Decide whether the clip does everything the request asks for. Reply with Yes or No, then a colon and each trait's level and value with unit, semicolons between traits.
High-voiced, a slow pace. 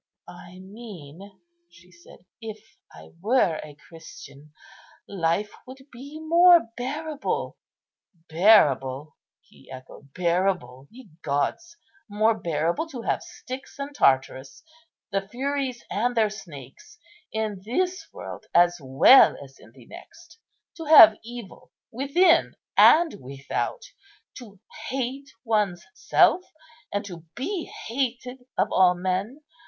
Yes: high, 210 Hz; slow, 115 wpm